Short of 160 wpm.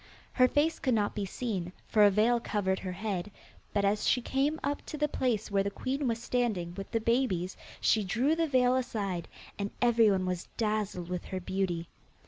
No: average, 195 wpm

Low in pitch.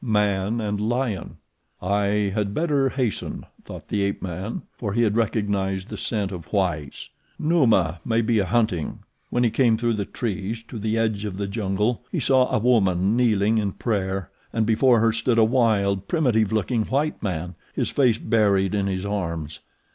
Yes: low, 105 Hz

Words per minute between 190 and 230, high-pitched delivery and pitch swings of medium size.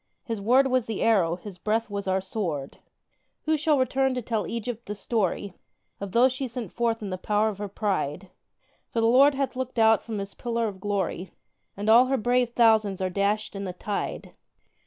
Yes: average, 200 wpm; high, 220 Hz; average, 3.5 semitones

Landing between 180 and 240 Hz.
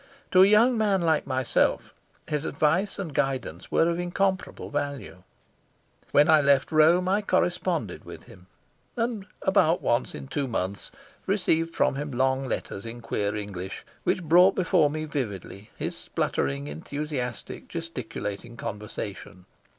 No: medium, 145 Hz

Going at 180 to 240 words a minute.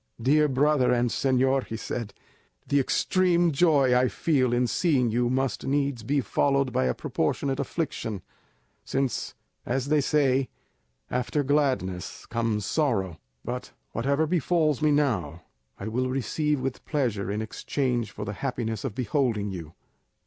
No: average, 140 wpm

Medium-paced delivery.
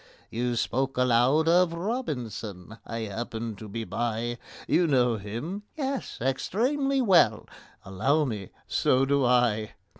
No: slow, 120 wpm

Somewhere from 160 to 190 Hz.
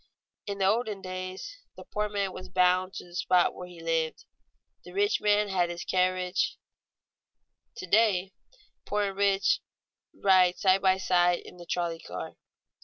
Yes: medium, 185 Hz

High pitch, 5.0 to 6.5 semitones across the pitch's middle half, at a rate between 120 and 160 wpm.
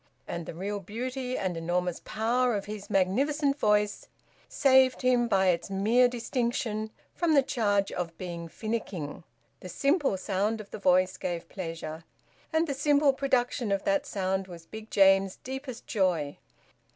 Yes: high, 210 Hz; wide, 5.4 semitones; average, 150 wpm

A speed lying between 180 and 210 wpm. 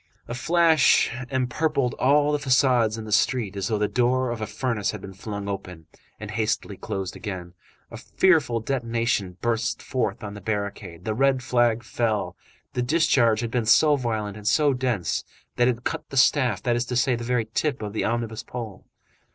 Yes: average, 190 wpm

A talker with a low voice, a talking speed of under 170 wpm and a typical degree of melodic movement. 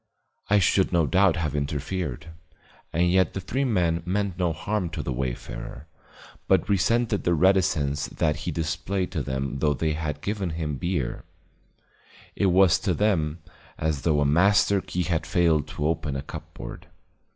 Yes: very low, 85 Hz; average, 160 wpm; average, 4.0 semitones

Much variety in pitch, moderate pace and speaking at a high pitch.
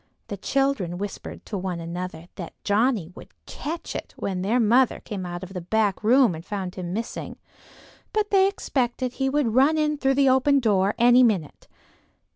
Yes: wide, 6.4 semitones; average, 180 wpm; high, 220 Hz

